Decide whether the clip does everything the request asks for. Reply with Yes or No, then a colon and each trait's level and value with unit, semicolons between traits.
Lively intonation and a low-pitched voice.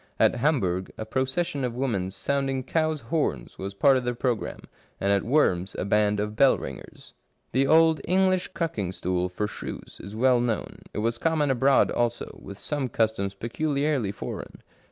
Yes: wide, 5.7 semitones; low, 120 Hz